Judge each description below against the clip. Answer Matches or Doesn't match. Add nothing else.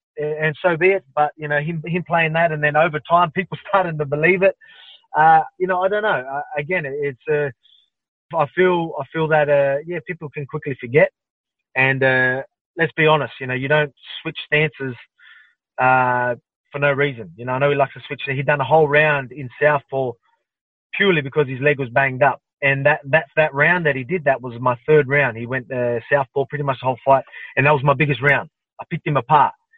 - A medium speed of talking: Doesn't match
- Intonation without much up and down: Doesn't match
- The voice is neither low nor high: Matches